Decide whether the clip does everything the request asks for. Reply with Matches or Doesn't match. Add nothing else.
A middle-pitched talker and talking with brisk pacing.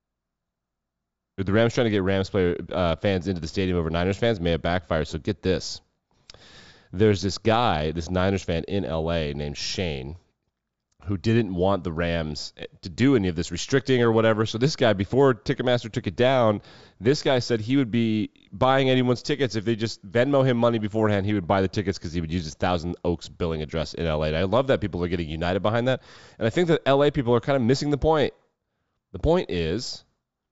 Doesn't match